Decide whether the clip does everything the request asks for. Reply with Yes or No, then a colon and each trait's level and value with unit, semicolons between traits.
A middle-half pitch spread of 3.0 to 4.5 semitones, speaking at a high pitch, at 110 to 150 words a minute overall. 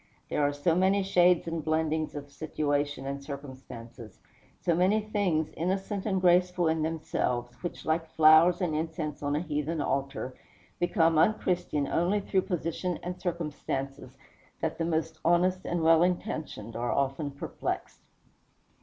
No: average, 3.6 semitones; medium, 160 Hz; average, 145 wpm